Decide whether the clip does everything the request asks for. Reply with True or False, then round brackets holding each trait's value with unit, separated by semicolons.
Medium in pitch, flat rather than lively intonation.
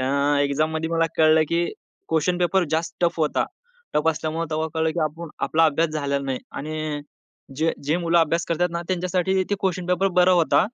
True (165 Hz; 1.9 semitones)